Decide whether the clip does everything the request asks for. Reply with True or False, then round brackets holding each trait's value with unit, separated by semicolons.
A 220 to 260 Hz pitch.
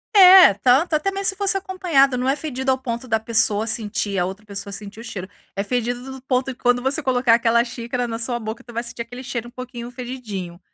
True (245 Hz)